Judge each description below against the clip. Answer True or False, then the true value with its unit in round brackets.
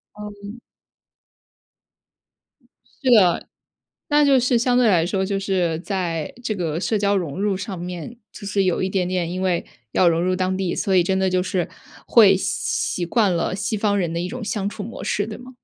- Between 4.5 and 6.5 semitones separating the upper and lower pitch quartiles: False (2.6 semitones)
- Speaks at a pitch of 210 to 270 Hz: False (190 Hz)